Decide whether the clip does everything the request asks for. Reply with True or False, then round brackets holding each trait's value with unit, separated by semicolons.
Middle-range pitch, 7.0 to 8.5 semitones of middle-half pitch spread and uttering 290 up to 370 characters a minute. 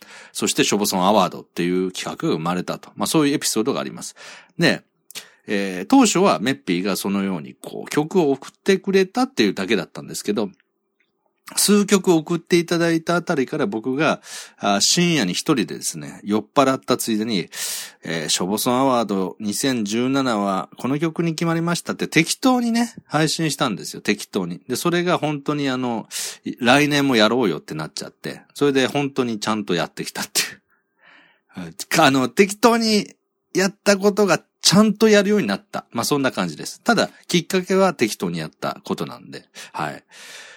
True (155 Hz; 7.6 semitones; 365 characters per minute)